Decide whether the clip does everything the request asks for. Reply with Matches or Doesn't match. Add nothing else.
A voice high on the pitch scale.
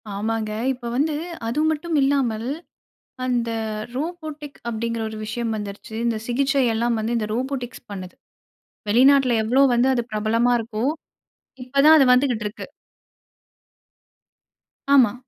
Matches